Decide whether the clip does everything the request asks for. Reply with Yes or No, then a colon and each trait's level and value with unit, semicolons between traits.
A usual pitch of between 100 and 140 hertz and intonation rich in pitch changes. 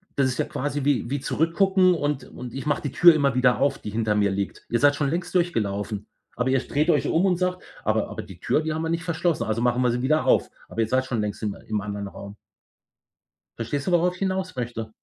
Yes: low, 135 Hz; wide, 6.2 semitones